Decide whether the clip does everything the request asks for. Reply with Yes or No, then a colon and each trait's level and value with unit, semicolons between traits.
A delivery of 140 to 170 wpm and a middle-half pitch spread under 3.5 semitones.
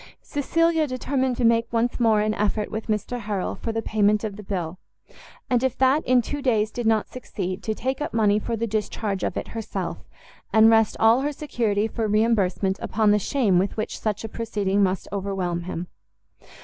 No: average, 195 wpm; average, 2.9 semitones